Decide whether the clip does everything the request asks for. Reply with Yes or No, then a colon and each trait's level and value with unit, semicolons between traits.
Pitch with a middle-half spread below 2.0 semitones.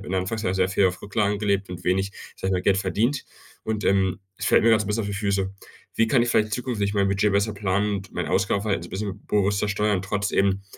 Yes: narrow, 1.6 semitones